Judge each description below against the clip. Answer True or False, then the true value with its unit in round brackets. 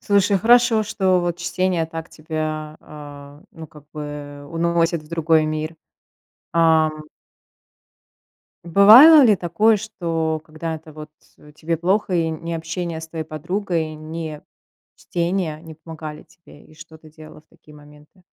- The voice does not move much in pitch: True (2.1 semitones)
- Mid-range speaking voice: True (160 Hz)